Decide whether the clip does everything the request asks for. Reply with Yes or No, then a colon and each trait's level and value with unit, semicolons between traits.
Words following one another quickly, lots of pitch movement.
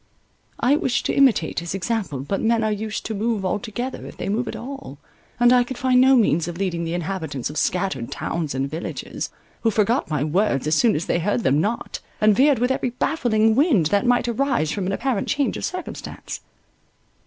Yes: fast, 210 wpm; wide, 6.3 semitones